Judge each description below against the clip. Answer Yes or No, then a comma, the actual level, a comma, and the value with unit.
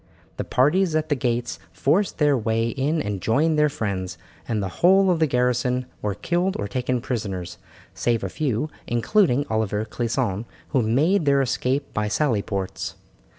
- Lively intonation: Yes, wide, 5.7 semitones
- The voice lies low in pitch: Yes, low, 125 Hz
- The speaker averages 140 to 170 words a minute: Yes, average, 165 wpm